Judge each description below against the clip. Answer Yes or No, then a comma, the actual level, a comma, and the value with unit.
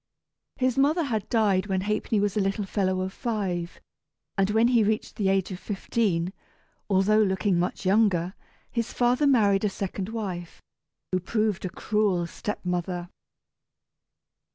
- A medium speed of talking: Yes, average, 150 wpm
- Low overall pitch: No, high, 200 Hz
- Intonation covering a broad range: No, average, 2.8 semitones